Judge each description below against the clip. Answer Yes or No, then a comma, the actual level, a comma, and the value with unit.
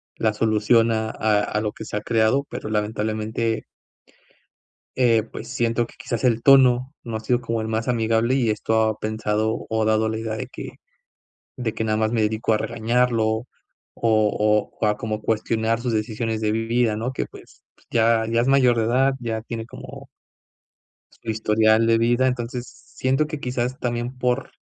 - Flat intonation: Yes, narrow, 1.8 semitones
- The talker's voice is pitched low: Yes, low, 115 Hz